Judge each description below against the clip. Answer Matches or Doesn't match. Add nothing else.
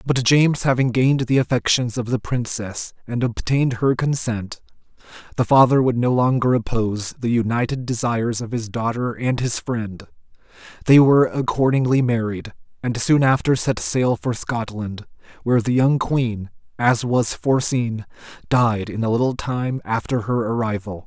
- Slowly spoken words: Doesn't match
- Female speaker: Doesn't match